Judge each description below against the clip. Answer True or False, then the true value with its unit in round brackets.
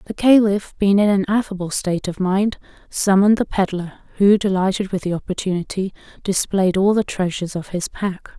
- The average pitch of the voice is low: False (195 Hz)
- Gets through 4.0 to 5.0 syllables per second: False (5.5 syllables/s)